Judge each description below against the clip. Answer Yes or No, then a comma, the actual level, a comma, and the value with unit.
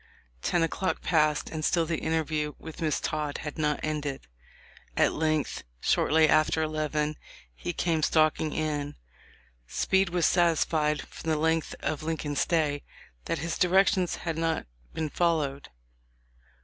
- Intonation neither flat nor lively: No, narrow, 1.5 semitones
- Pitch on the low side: No, medium, 155 Hz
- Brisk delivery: No, slow, 135 wpm